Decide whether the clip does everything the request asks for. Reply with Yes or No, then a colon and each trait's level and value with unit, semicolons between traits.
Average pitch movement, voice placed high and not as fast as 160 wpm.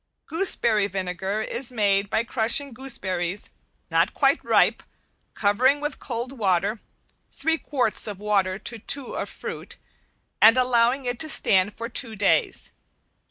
Yes: average, 4.2 semitones; high, 225 Hz; slow, 135 wpm